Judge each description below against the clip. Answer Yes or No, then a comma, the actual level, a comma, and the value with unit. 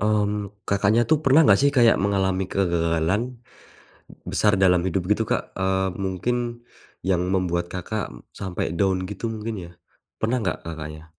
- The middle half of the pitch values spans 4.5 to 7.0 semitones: No, average, 3.2 semitones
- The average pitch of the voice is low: Yes, very low, 95 Hz